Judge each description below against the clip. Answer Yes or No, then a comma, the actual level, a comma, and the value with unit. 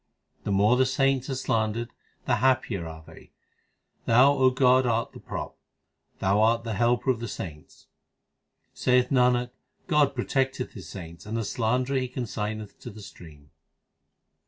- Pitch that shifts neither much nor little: Yes, average, 3.6 semitones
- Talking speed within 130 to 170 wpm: Yes, average, 155 wpm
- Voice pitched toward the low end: Yes, low, 120 Hz